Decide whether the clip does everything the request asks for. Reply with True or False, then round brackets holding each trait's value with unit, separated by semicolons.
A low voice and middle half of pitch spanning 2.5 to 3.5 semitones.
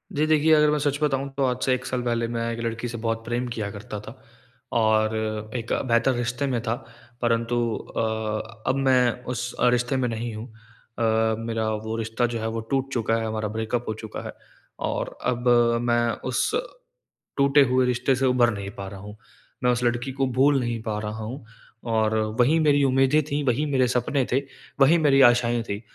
True (120 Hz; 2.8 semitones)